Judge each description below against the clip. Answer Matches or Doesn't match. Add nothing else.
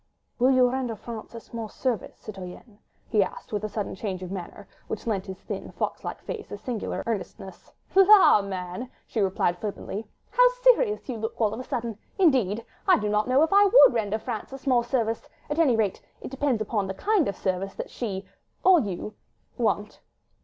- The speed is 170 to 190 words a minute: Matches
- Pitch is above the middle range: Matches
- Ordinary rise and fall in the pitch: Matches